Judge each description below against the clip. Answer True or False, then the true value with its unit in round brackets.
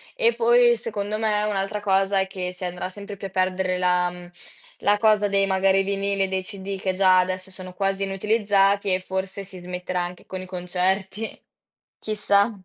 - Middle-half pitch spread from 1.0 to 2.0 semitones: True (1.6 semitones)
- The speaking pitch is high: True (195 Hz)